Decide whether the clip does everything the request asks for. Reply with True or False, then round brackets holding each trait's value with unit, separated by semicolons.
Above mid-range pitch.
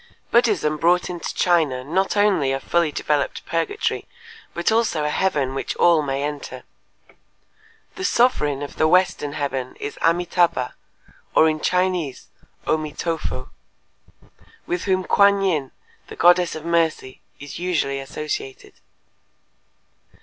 False (165 Hz)